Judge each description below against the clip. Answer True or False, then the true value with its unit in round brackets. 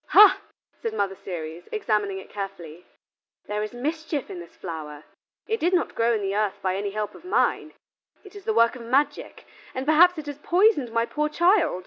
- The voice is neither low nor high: False (230 Hz)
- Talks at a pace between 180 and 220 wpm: True (195 wpm)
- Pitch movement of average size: False (8.7 semitones)